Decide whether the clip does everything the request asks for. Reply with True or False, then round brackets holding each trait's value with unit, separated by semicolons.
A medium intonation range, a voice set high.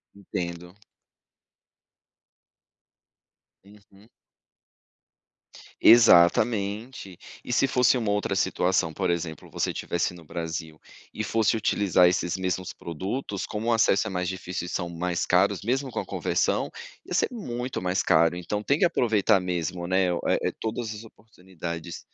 False (4.1 semitones; 95 Hz)